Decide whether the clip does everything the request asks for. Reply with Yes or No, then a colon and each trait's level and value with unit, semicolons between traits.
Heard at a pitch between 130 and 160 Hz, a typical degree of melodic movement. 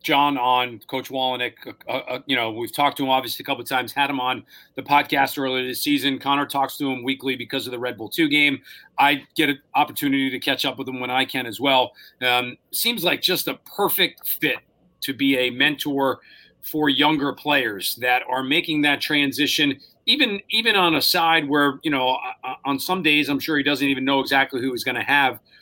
No: low, 135 Hz; narrow, 2.0 semitones